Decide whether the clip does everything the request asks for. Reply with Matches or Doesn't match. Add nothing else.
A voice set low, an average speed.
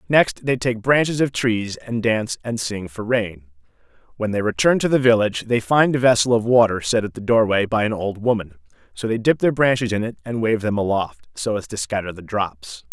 Doesn't match